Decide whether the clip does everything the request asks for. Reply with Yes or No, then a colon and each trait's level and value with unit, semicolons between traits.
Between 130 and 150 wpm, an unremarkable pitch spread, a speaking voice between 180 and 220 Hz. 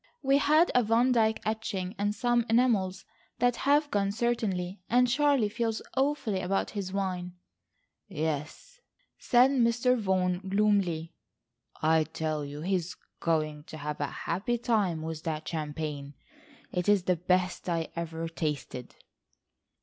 No: average, 140 wpm; wide, 6.3 semitones; high, 190 Hz